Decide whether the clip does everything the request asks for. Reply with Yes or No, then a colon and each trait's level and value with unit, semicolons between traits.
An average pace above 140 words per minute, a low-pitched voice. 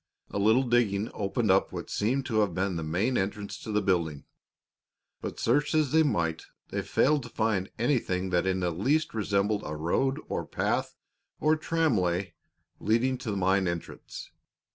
Yes: average, 170 wpm; low, 105 Hz